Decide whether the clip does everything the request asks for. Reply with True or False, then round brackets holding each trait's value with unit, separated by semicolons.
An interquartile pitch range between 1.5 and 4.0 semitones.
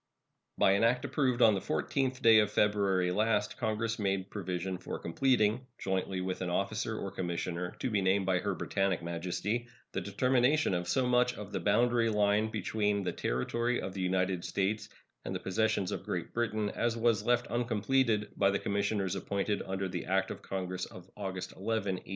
True (3.3 semitones)